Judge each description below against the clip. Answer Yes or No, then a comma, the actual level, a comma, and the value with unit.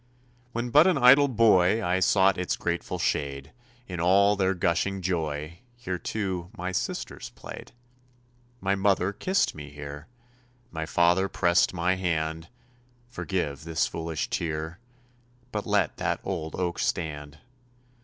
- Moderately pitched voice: No, very low, 90 Hz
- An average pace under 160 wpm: Yes, slow, 135 wpm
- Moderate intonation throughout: Yes, average, 3.5 semitones